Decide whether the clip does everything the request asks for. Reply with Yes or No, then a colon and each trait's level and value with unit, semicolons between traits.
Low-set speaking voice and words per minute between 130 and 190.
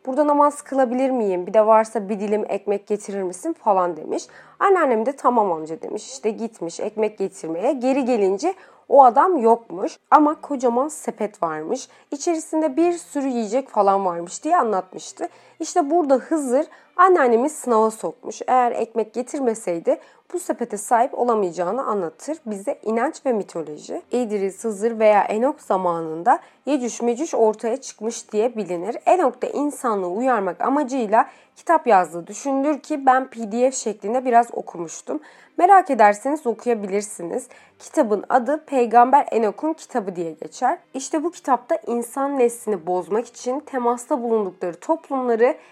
No: high, 240 Hz; average, 135 wpm